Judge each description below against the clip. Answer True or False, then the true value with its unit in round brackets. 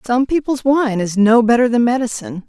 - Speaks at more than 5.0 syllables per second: True (5.6 syllables/s)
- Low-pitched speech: False (235 Hz)